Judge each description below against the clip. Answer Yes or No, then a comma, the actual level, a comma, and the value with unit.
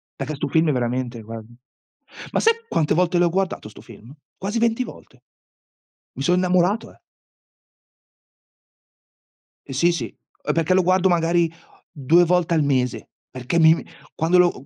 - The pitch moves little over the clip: No, wide, 5.6 semitones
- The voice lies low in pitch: No, medium, 165 Hz